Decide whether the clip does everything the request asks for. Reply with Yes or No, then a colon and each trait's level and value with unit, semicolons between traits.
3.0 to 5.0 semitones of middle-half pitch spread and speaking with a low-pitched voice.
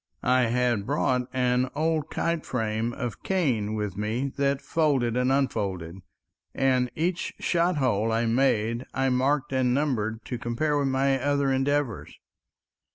Yes: average, 3.6 semitones; low, 130 Hz